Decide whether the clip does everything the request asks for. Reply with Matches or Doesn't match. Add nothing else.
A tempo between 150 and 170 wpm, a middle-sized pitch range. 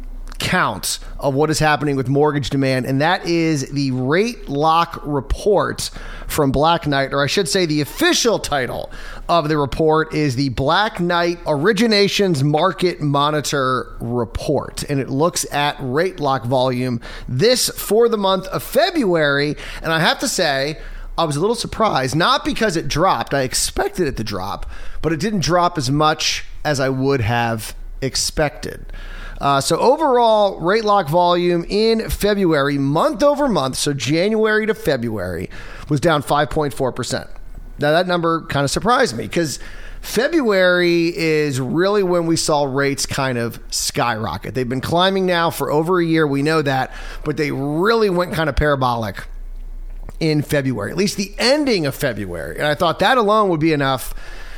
Matches